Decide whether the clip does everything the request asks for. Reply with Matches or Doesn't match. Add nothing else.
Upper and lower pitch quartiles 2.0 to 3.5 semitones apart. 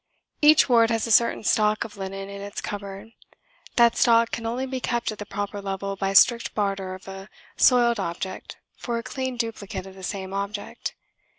Matches